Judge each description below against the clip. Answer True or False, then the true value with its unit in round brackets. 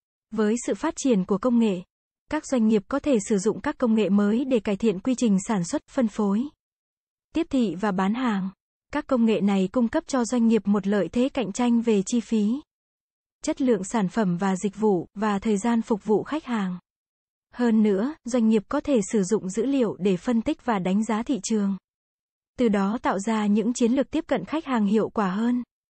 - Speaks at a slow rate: False (220 wpm)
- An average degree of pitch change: True (3.4 semitones)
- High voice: True (225 Hz)